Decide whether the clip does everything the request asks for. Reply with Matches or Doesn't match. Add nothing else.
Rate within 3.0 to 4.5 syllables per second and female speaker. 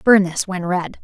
Matches